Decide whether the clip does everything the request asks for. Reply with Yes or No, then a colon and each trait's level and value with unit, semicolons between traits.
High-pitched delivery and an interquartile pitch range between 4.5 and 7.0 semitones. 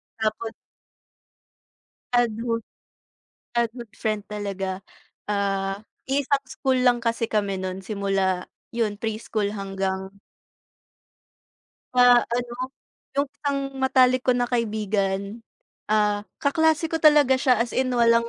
No: high, 230 Hz; average, 3.8 semitones